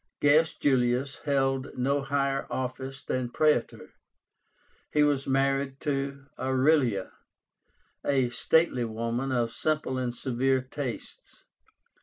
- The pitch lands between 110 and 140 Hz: Yes, low, 135 Hz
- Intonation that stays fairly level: Yes, narrow, 1.8 semitones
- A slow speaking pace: Yes, slow, 105 wpm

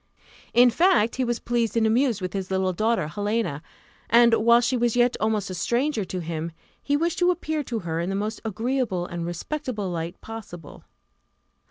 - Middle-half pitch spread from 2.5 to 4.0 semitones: No, average, 4.7 semitones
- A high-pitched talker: Yes, high, 220 Hz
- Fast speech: No, average, 185 wpm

